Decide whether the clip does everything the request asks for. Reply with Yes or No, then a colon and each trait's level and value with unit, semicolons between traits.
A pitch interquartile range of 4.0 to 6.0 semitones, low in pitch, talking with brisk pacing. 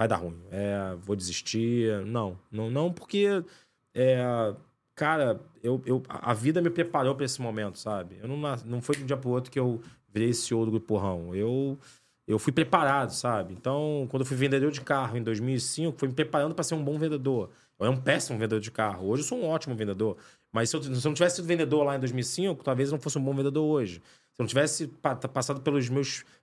Yes: average, 4.6 semitones; low, 130 Hz; fast, 225 wpm